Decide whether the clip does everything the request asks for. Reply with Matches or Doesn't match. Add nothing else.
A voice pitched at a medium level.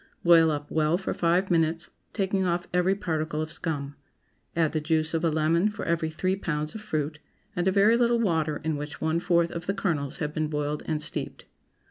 Matches